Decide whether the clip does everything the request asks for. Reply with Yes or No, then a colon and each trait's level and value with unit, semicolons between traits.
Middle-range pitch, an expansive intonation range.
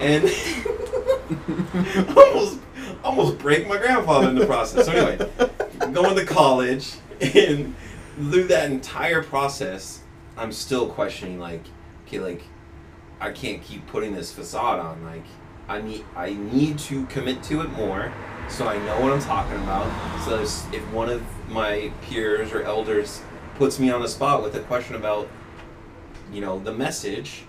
No: low, 115 Hz; wide, 7.9 semitones